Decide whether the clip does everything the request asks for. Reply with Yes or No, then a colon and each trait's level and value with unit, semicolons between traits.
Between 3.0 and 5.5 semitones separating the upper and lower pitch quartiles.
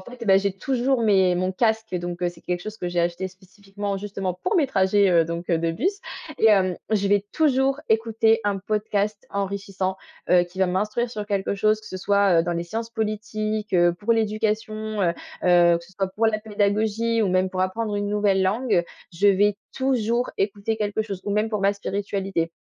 No: narrow, 2.6 semitones